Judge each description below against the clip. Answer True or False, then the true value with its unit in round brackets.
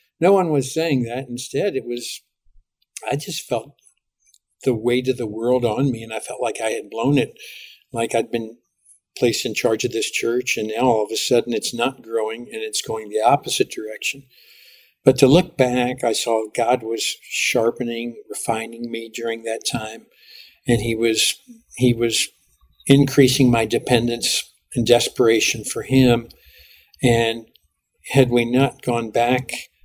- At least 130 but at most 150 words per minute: False (165 wpm)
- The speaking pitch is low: True (120 Hz)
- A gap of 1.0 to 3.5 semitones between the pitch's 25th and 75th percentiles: True (2.5 semitones)